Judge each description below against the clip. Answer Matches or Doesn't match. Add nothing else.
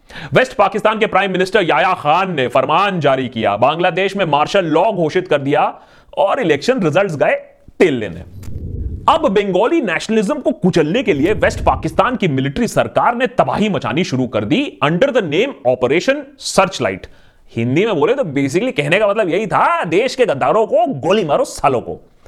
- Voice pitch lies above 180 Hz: Matches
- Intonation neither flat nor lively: Doesn't match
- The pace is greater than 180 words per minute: Doesn't match